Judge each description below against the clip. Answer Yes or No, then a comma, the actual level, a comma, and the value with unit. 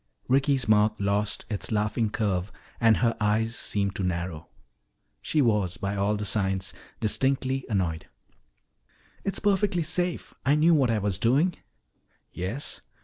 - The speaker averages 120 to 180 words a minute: Yes, average, 140 wpm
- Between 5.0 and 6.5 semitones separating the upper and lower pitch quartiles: Yes, average, 5.3 semitones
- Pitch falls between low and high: No, low, 105 Hz